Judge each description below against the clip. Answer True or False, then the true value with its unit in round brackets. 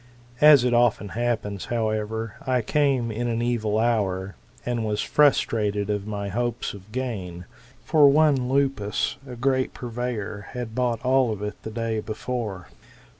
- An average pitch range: True (3.0 semitones)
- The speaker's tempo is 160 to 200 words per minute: False (150 wpm)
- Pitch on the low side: True (115 Hz)